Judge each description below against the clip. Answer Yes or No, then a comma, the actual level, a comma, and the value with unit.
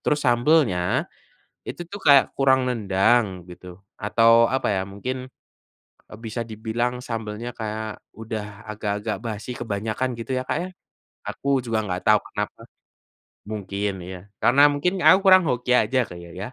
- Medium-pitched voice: No, low, 115 Hz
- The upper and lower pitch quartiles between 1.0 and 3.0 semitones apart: No, average, 3.8 semitones